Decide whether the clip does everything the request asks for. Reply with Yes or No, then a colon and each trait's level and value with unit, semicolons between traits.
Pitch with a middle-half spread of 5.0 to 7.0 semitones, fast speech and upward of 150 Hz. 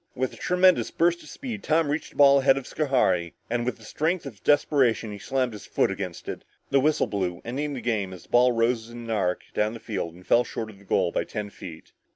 No: average, 5.3 semitones; fast, 245 wpm; low, 120 Hz